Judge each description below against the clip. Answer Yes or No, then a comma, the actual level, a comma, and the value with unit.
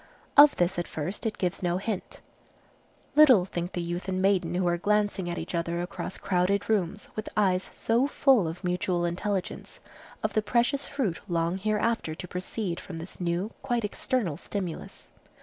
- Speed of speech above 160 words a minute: Yes, average, 170 wpm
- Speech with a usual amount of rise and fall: Yes, average, 3.4 semitones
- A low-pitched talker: No, medium, 185 Hz